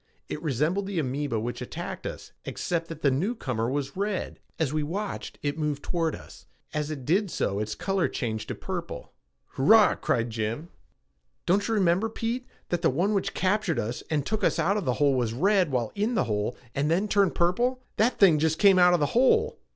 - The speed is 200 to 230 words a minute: Yes, fast, 205 wpm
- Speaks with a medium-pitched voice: Yes, medium, 165 Hz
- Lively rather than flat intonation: Yes, wide, 6.5 semitones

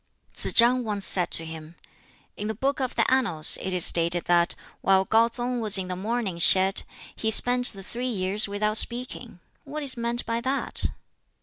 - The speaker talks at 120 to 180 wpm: No, average, 190 wpm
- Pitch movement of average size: Yes, average, 4.6 semitones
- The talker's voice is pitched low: No, high, 215 Hz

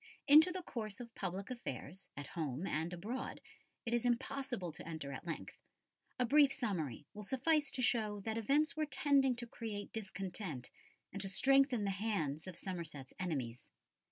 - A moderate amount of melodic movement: No, wide, 6.8 semitones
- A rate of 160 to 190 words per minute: Yes, average, 165 wpm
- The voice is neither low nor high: No, high, 210 Hz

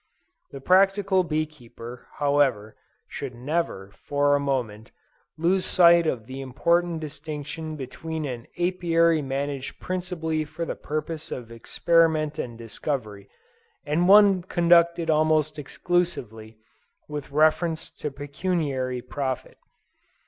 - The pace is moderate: No, slow, 110 wpm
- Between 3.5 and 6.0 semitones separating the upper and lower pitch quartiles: Yes, average, 4.2 semitones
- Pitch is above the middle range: No, medium, 150 Hz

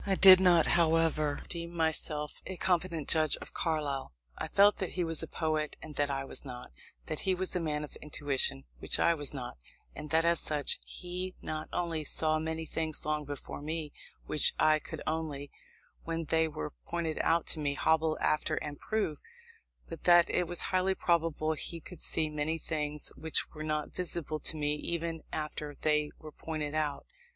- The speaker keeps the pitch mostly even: Yes, narrow, 2.1 semitones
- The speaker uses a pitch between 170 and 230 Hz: No, medium, 155 Hz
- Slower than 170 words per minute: No, average, 185 wpm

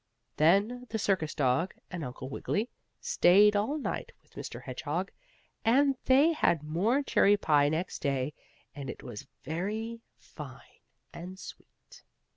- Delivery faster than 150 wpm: No, slow, 135 wpm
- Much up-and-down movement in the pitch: Yes, wide, 7.1 semitones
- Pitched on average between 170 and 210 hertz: Yes, high, 190 Hz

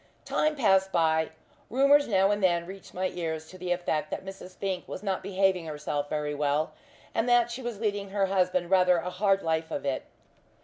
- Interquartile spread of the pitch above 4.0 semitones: No, average, 3.4 semitones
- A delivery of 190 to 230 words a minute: Yes, average, 195 wpm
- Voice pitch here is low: No, medium, 185 Hz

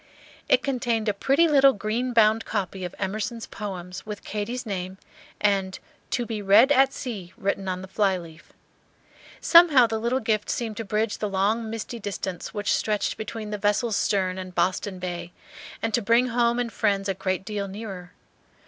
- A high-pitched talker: Yes, high, 210 Hz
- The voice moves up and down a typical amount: Yes, average, 3.3 semitones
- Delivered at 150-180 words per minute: Yes, average, 175 wpm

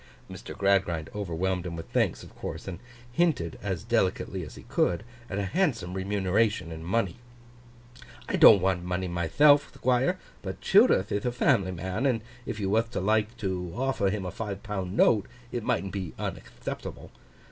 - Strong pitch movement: No, average, 3.6 semitones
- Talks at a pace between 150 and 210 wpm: Yes, average, 170 wpm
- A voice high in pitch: No, very low, 95 Hz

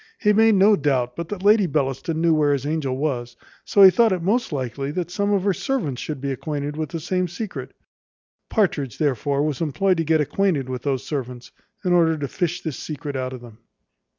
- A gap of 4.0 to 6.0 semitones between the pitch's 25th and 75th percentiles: Yes, average, 5.1 semitones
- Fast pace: Yes, fast, 210 wpm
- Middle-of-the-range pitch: Yes, medium, 155 Hz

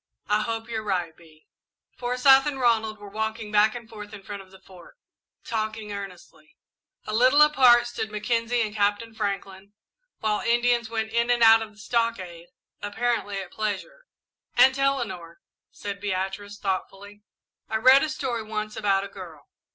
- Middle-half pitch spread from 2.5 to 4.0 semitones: Yes, average, 2.8 semitones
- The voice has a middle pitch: No, high, 215 Hz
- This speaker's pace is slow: No, average, 160 wpm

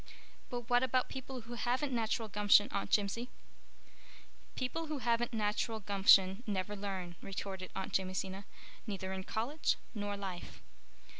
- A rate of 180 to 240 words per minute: No, slow, 135 wpm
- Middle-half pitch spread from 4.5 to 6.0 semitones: No, average, 3.9 semitones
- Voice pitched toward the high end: Yes, high, 210 Hz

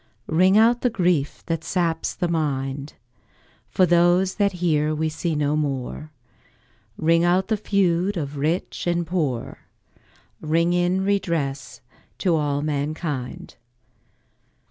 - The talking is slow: Yes, slow, 120 wpm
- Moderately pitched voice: Yes, medium, 165 Hz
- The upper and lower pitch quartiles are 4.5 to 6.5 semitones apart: No, average, 3.3 semitones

